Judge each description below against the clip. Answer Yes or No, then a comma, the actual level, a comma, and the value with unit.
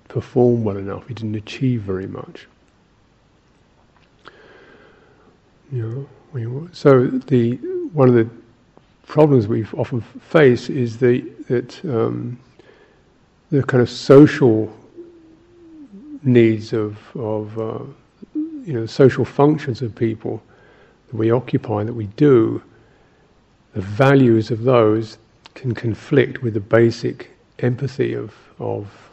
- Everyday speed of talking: No, slow, 115 wpm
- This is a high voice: No, low, 120 Hz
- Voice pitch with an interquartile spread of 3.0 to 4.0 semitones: Yes, average, 3.5 semitones